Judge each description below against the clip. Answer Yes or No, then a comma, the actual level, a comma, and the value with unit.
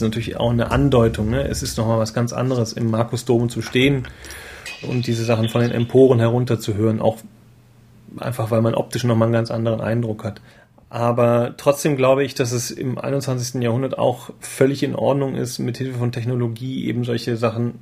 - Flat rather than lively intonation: Yes, narrow, 1.8 semitones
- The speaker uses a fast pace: No, average, 180 wpm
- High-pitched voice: No, low, 120 Hz